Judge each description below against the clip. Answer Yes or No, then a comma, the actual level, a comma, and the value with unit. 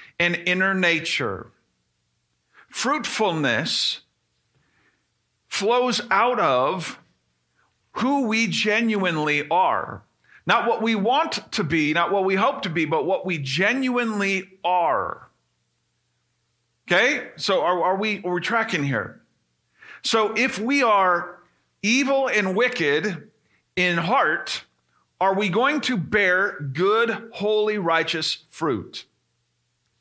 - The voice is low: No, high, 190 Hz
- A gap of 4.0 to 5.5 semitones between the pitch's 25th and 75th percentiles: Yes, average, 5.2 semitones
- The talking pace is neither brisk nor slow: No, slow, 110 wpm